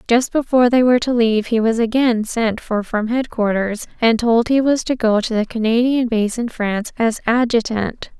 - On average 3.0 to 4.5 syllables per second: No, 5.0 syllables/s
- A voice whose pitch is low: No, high, 230 Hz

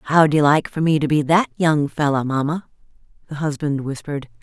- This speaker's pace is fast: No, average, 190 wpm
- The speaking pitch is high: No, medium, 150 Hz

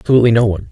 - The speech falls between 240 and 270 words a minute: Yes, fast, 250 wpm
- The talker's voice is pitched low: Yes, low, 115 Hz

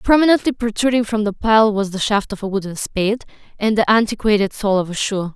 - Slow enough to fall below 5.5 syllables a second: No, 5.9 syllables/s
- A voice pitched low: No, high, 210 Hz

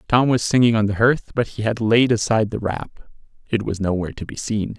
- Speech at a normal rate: No, fast, 225 wpm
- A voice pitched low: Yes, low, 110 Hz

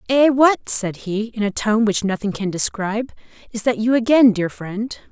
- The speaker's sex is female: Yes, female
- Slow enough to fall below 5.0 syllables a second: Yes, 4.7 syllables/s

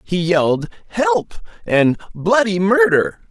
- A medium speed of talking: No, slow, 110 wpm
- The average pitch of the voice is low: No, medium, 175 Hz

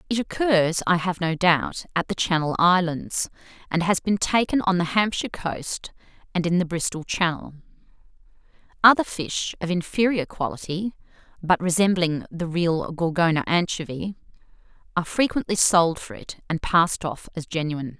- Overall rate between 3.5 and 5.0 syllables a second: Yes, 4.9 syllables/s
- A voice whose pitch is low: No, medium, 175 Hz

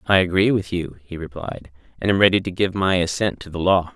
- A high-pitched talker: No, very low, 90 Hz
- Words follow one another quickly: Yes, fast, 245 wpm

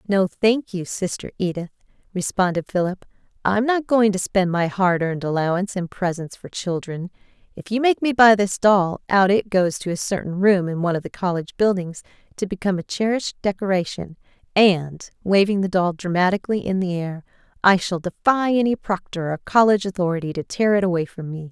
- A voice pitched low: No, high, 190 Hz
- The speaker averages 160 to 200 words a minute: Yes, average, 185 wpm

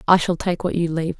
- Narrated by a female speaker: Yes, female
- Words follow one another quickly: Yes, fast, 300 wpm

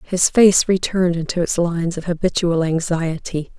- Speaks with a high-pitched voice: No, medium, 175 Hz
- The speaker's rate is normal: Yes, average, 150 wpm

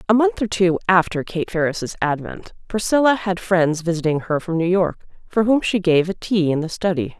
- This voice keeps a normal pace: No, fast, 210 wpm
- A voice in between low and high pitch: Yes, medium, 180 Hz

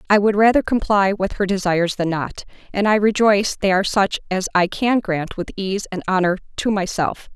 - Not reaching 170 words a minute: No, fast, 205 wpm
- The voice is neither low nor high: No, high, 195 Hz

